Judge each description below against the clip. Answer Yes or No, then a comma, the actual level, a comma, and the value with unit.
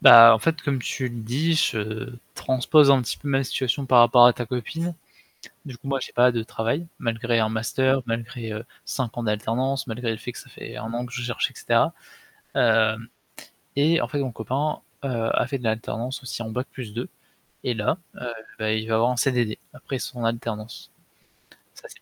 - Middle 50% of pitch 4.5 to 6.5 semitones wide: No, narrow, 2.6 semitones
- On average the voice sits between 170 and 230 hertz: No, low, 120 Hz